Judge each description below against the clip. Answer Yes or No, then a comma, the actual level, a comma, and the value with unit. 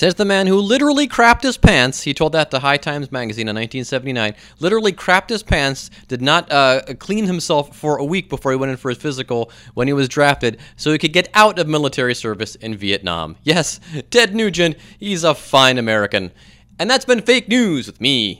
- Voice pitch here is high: No, medium, 140 Hz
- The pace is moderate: No, fast, 210 wpm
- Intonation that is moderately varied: No, wide, 7.0 semitones